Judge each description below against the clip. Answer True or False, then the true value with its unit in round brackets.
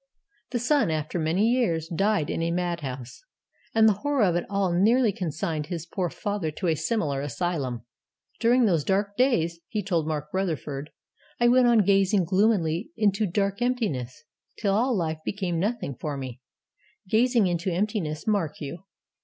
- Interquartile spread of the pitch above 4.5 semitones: True (5.1 semitones)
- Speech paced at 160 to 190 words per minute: True (165 wpm)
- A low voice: False (180 Hz)